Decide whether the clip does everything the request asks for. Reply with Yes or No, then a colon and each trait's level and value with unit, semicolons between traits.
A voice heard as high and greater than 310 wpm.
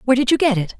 Yes: high, 245 Hz; fast, 375 wpm